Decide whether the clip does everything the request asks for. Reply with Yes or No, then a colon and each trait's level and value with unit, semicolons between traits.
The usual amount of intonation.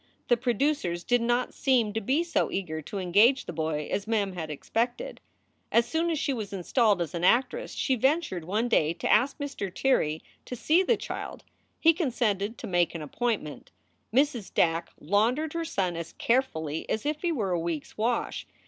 No: wide, 7.3 semitones